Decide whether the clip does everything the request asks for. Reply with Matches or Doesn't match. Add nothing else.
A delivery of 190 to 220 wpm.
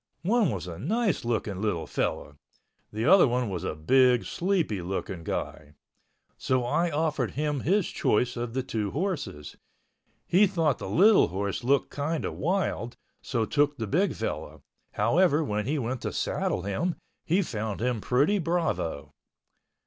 Doesn't match